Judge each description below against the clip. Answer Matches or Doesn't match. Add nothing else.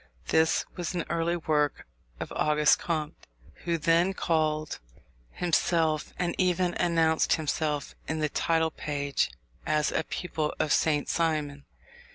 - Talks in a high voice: Doesn't match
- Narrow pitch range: Matches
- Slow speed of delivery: Matches